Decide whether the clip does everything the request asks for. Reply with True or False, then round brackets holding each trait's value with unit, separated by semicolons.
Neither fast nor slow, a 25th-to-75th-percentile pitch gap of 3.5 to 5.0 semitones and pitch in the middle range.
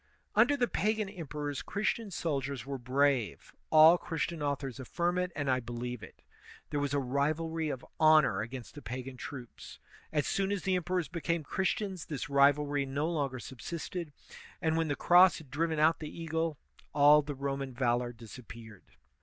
True (165 wpm; 3.9 semitones; 145 Hz)